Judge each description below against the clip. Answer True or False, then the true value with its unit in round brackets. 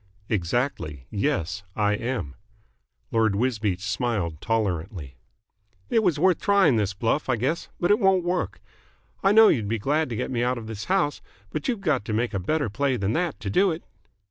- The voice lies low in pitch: True (120 Hz)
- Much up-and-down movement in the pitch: True (7.5 semitones)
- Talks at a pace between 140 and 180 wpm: False (190 wpm)